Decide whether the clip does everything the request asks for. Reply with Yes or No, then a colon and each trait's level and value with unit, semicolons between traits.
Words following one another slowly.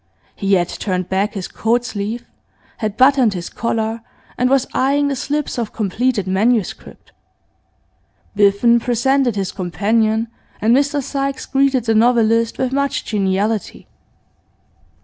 Yes: slow, 130 wpm